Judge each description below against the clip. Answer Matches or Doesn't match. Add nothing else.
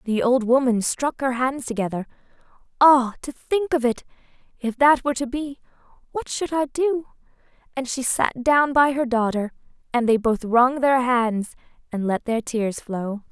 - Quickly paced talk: Doesn't match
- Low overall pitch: Doesn't match